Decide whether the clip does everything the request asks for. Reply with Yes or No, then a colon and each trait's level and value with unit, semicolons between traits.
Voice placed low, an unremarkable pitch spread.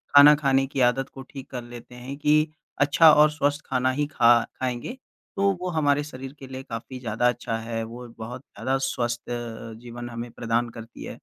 Yes: low, 130 Hz; average, 3.1 semitones